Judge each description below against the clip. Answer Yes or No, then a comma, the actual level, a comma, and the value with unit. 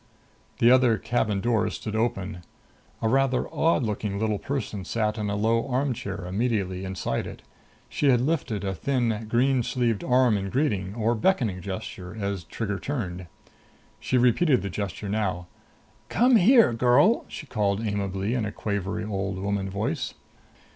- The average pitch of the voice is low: Yes, low, 110 Hz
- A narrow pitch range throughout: No, average, 4.0 semitones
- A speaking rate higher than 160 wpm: No, average, 155 wpm